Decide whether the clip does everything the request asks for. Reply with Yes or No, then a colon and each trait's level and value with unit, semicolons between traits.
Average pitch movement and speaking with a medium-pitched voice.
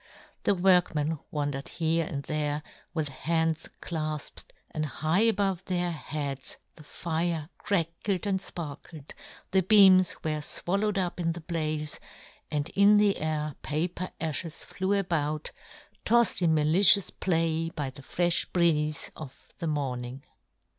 Yes: average, 3.3 semitones; medium, 165 Hz